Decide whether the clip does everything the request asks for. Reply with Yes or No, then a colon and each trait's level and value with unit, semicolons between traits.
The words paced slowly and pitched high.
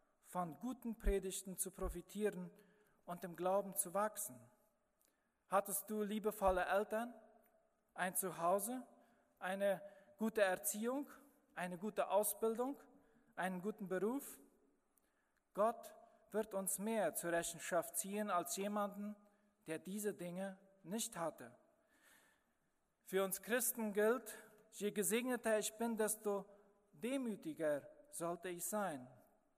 Yes: slow, 105 wpm; high, 205 Hz